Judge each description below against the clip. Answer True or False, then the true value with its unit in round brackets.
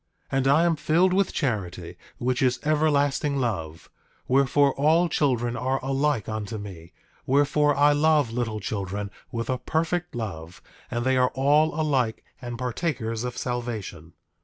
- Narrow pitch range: False (4.8 semitones)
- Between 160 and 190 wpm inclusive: False (150 wpm)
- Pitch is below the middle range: True (130 Hz)